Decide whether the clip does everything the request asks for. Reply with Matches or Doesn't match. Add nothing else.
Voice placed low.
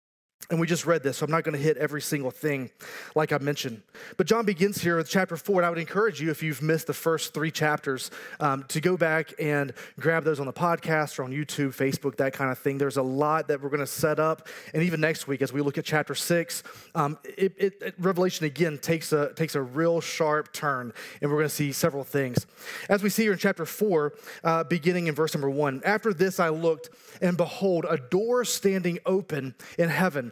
Doesn't match